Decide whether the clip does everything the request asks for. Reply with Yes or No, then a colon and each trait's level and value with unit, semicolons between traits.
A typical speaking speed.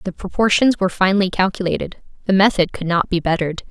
Yes: average, 180 wpm